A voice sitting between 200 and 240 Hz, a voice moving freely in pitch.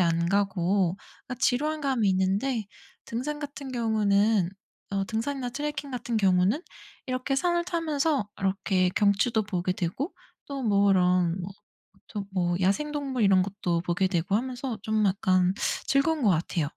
Yes: high, 210 Hz; wide, 6.3 semitones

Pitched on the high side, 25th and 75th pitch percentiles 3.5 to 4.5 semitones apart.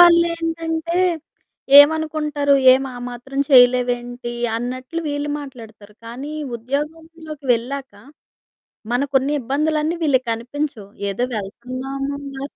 Yes: very high, 275 Hz; average, 3.8 semitones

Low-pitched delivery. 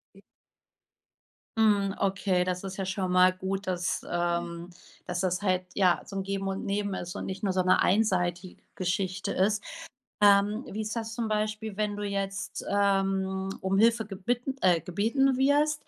No: high, 195 Hz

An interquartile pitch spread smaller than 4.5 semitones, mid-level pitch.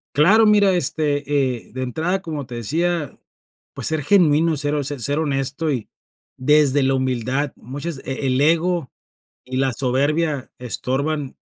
Yes: average, 3.3 semitones; medium, 145 Hz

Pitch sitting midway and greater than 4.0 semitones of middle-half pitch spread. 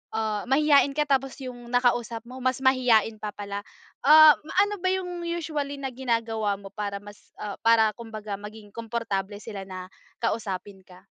No: high, 230 Hz; average, 4.6 semitones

